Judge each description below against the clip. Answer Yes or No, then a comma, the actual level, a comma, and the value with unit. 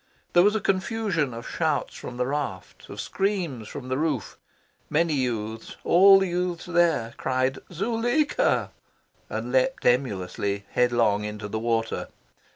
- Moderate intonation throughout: No, wide, 8.1 semitones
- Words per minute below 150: Yes, average, 140 wpm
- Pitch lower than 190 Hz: Yes, low, 135 Hz